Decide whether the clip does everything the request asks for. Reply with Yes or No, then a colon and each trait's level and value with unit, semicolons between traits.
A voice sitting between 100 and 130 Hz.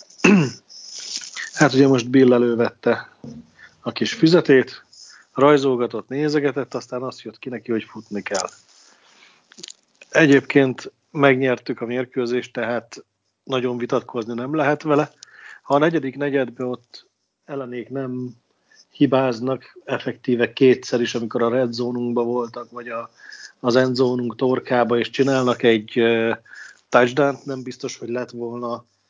Yes: low, 125 Hz